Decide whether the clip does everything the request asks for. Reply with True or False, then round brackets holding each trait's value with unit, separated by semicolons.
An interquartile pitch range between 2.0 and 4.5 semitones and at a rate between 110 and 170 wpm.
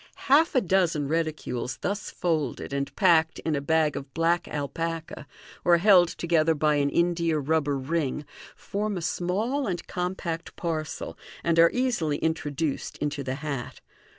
True (2.9 semitones; 150 wpm)